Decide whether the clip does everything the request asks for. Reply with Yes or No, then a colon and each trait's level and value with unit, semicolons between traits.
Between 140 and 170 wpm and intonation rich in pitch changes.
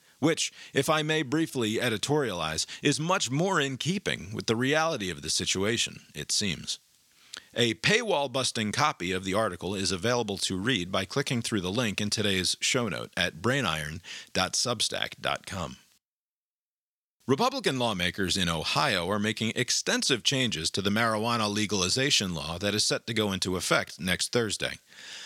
Yes: average, 150 wpm; wide, 5.9 semitones